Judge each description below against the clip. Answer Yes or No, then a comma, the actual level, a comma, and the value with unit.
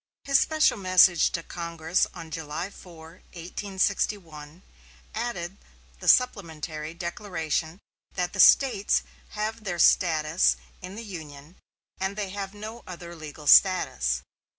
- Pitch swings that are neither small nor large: Yes, average, 3.8 semitones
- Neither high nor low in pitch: Yes, medium, 180 Hz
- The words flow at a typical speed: No, slow, 120 wpm